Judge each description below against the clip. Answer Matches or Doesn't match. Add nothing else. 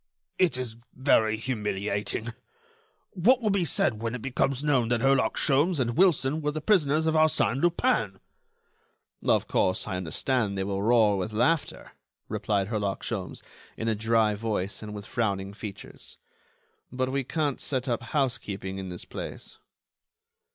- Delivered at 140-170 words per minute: Matches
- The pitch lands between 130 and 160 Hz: Doesn't match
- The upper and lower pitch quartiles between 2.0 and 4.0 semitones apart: Doesn't match